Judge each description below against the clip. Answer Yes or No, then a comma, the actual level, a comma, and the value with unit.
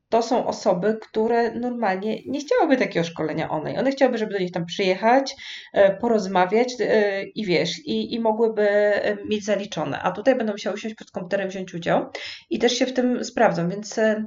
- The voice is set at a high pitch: Yes, high, 215 Hz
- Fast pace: Yes, fast, 170 wpm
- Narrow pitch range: No, average, 3.2 semitones